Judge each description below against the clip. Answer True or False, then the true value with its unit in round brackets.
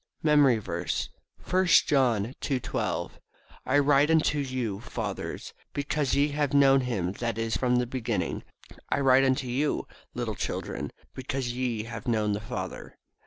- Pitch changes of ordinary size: True (3.6 semitones)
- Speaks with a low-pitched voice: True (130 Hz)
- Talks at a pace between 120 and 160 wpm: True (150 wpm)